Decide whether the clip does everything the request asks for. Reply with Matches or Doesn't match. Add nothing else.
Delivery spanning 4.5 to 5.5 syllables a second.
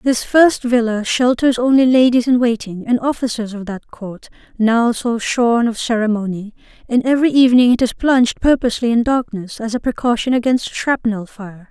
Matches